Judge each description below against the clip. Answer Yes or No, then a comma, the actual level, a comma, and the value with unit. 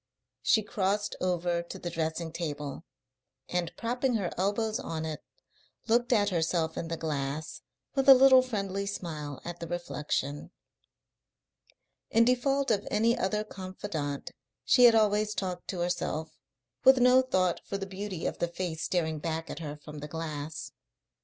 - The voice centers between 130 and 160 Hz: No, medium, 180 Hz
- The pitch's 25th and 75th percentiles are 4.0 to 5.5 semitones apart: Yes, average, 5.0 semitones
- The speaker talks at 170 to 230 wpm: No, average, 155 wpm